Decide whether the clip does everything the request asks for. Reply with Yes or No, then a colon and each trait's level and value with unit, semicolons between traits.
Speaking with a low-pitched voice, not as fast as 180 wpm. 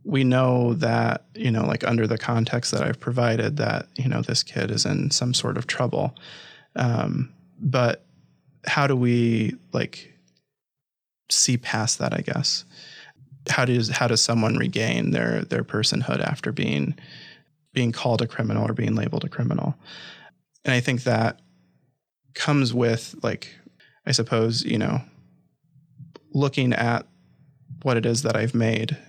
Yes: low, 120 Hz; average, 150 wpm